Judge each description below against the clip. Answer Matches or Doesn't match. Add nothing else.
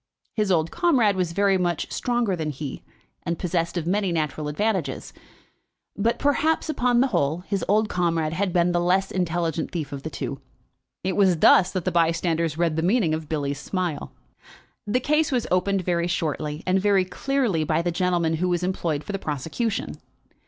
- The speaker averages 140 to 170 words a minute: Doesn't match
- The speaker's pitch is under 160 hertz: Doesn't match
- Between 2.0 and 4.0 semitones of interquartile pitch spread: Matches